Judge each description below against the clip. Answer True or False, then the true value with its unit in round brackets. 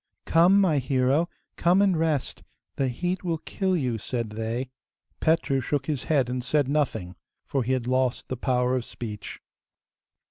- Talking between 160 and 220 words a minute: True (165 wpm)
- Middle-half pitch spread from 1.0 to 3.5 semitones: False (4.6 semitones)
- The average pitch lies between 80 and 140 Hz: True (135 Hz)